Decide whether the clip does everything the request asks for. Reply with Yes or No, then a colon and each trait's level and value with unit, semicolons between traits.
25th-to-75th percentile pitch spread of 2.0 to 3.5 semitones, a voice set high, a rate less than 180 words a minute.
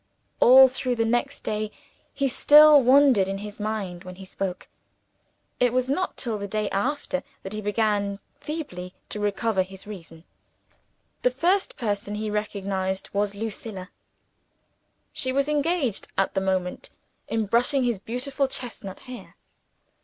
No: average, 4.7 semitones; high, 215 Hz; average, 145 wpm